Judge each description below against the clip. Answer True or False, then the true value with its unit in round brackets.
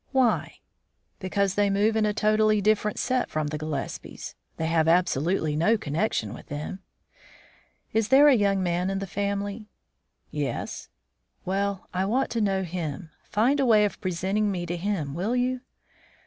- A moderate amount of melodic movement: True (3.7 semitones)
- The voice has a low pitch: False (200 Hz)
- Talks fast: False (160 wpm)